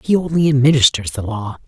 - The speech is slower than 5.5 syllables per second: No, 5.9 syllables/s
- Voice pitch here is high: No, low, 130 Hz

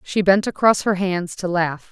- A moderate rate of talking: No, fast, 220 wpm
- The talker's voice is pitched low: No, medium, 185 Hz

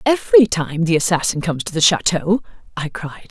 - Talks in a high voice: No, medium, 180 Hz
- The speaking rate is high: No, average, 180 wpm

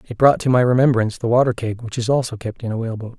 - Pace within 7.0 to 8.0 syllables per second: Yes, 7.2 syllables/s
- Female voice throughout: No, male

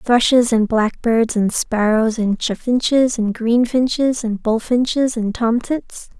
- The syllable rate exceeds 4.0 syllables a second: No, 3.8 syllables/s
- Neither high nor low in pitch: No, high, 235 Hz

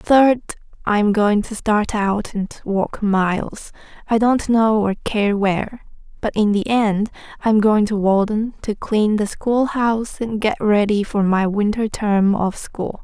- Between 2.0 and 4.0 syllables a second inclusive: Yes, 3.8 syllables/s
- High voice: Yes, high, 210 Hz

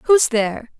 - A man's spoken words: No, female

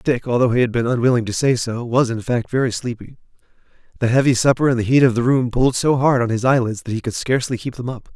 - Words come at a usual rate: No, fast, 265 wpm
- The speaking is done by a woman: No, male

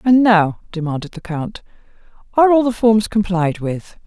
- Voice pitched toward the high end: Yes, high, 200 Hz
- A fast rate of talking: No, average, 160 wpm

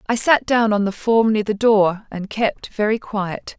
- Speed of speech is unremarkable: No, fast, 220 wpm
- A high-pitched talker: Yes, high, 215 Hz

